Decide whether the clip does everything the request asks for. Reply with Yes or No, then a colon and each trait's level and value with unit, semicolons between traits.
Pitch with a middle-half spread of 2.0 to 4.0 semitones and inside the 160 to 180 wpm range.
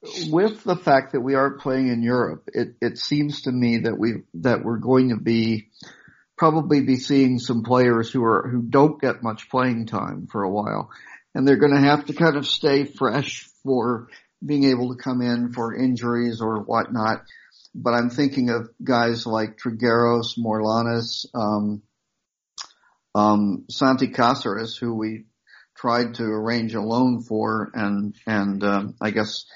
Yes: average, 2.9 semitones; average, 165 wpm